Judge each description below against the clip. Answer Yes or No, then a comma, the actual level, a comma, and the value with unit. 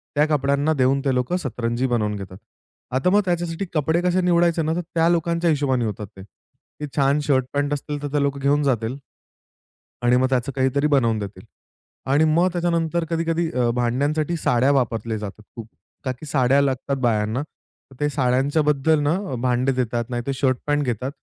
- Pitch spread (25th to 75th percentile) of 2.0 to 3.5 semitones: No, average, 4.0 semitones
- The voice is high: No, medium, 140 Hz